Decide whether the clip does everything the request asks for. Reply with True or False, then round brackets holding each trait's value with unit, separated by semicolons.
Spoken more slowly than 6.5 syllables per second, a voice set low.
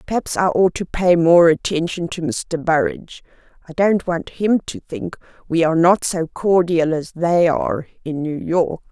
False (4.6 syllables/s; 170 Hz)